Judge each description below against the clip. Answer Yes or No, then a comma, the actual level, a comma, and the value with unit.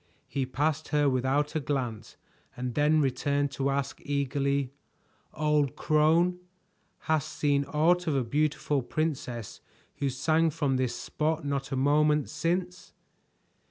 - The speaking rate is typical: No, slow, 130 wpm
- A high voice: No, medium, 145 Hz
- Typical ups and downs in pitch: No, narrow, 2.2 semitones